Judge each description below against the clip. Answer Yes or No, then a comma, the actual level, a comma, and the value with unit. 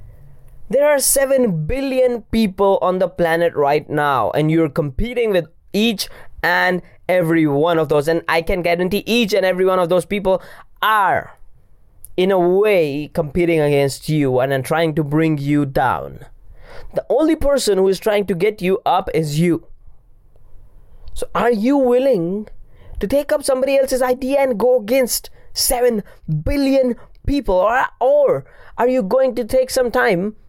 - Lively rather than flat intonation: Yes, wide, 8.1 semitones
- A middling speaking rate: Yes, average, 155 wpm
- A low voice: No, medium, 185 Hz